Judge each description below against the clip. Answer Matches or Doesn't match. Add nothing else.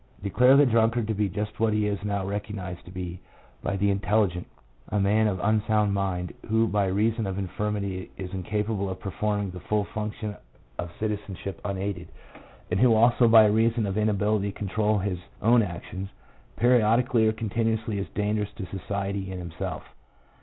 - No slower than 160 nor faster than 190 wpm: Matches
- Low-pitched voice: Matches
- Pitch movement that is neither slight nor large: Doesn't match